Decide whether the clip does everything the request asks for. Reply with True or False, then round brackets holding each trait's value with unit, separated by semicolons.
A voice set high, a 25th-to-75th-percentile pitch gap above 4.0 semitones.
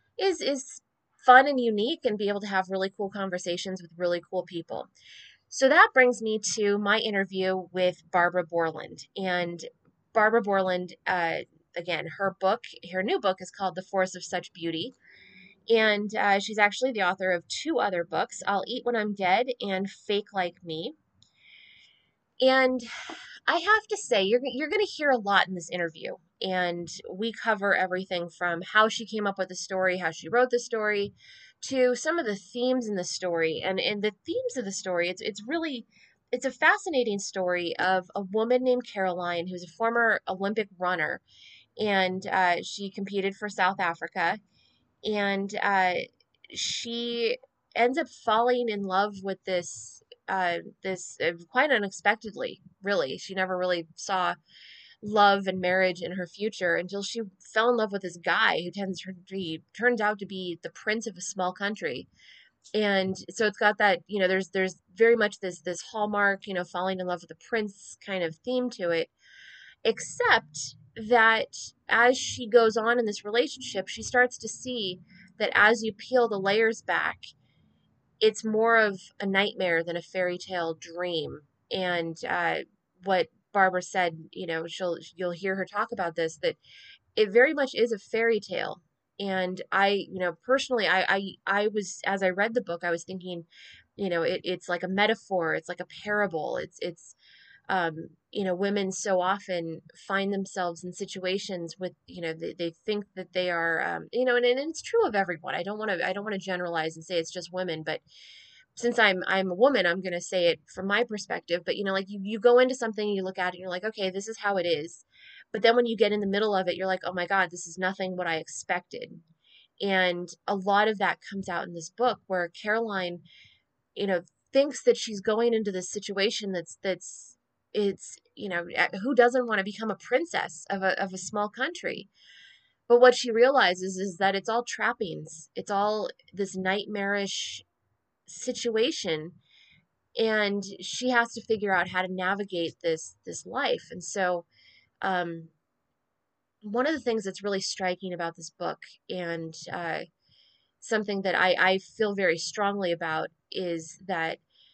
False (195 Hz; 3.7 semitones)